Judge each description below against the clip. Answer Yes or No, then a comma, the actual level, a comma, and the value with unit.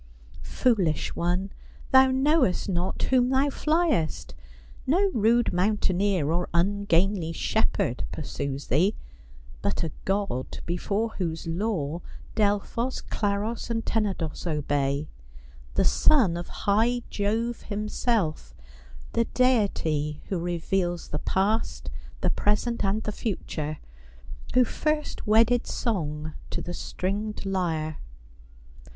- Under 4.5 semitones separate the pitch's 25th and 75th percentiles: No, wide, 5.4 semitones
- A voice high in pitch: Yes, high, 200 Hz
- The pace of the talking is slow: Yes, slow, 110 wpm